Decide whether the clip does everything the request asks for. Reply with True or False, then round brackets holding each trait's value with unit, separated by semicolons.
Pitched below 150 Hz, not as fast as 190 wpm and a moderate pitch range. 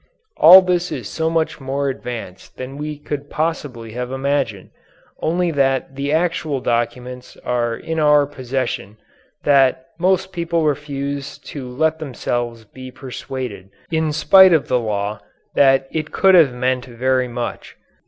True (135 Hz; 145 wpm; 4.0 semitones)